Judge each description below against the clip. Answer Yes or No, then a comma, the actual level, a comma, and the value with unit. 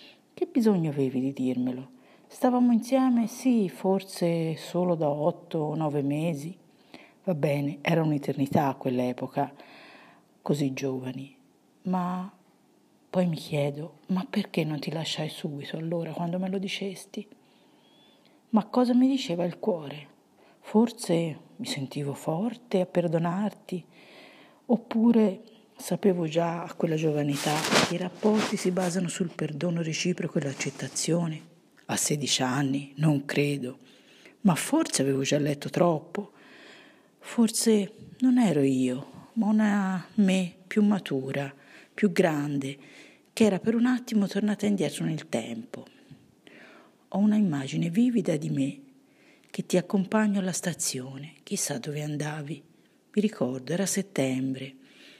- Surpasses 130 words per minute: No, average, 125 wpm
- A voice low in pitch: No, medium, 175 Hz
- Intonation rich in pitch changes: Yes, wide, 6.3 semitones